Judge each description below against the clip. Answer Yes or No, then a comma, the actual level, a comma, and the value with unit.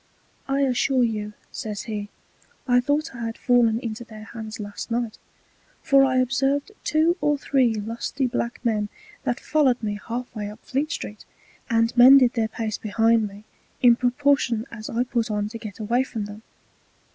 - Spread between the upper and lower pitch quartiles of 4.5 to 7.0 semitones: No, average, 3.1 semitones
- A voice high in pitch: Yes, high, 235 Hz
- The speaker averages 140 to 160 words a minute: No, average, 170 wpm